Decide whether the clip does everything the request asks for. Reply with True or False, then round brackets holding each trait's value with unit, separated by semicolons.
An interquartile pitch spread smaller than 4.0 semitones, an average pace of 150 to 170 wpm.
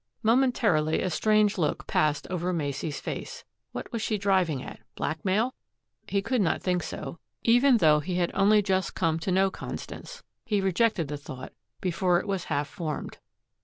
False (5.0 semitones; 165 wpm)